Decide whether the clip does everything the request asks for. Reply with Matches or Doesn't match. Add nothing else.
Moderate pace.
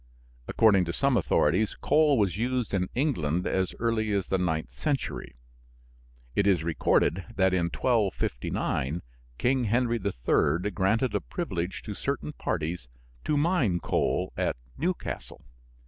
Doesn't match